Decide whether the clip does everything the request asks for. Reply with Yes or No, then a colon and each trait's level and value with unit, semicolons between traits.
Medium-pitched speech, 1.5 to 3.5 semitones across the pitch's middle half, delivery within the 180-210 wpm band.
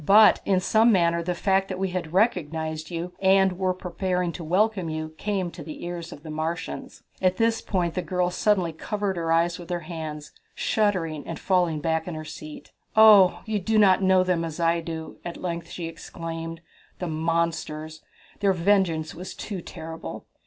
Yes: medium, 175 Hz; narrow, 2.6 semitones; average, 185 wpm